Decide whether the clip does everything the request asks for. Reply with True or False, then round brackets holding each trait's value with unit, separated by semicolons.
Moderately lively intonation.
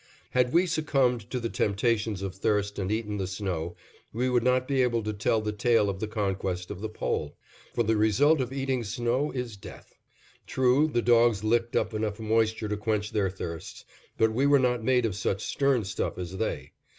True (3.4 semitones)